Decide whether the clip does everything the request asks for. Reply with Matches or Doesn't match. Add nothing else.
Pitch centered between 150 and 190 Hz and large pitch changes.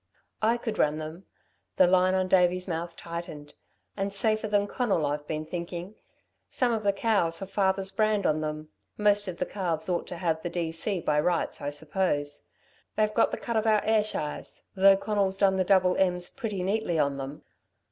Doesn't match